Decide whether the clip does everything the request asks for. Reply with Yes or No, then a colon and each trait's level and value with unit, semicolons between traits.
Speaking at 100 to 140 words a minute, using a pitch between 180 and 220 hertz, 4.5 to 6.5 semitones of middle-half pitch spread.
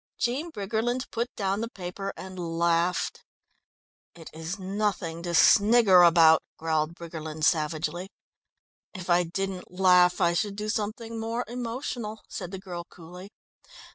No: slow, 135 wpm; medium, 185 Hz; average, 3.9 semitones